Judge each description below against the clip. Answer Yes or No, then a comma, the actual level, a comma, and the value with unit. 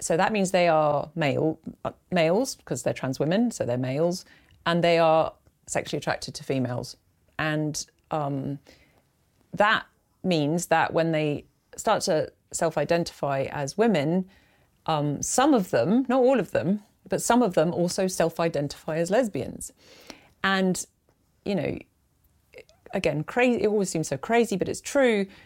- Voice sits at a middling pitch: Yes, medium, 170 Hz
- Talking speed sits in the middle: Yes, average, 145 wpm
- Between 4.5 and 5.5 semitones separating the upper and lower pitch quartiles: Yes, average, 5.1 semitones